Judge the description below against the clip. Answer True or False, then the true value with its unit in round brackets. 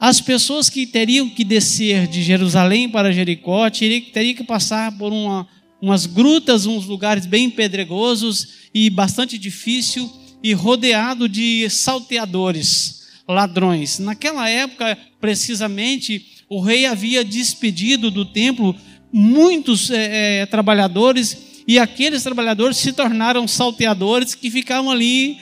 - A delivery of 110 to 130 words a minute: True (120 wpm)